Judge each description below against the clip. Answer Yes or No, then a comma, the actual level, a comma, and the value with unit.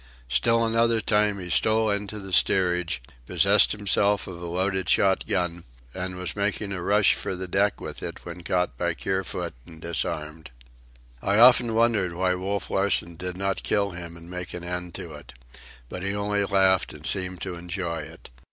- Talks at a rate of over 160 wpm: Yes, average, 180 wpm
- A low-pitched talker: Yes, very low, 95 Hz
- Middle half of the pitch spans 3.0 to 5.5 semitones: No, narrow, 2.5 semitones